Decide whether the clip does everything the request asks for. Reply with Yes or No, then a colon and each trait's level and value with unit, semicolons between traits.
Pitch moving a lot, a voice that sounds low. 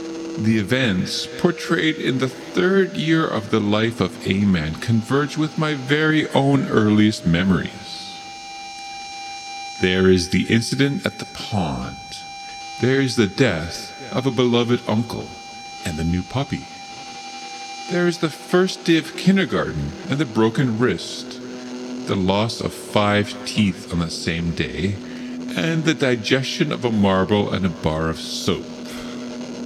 Yes: wide, 7.3 semitones; low, 125 Hz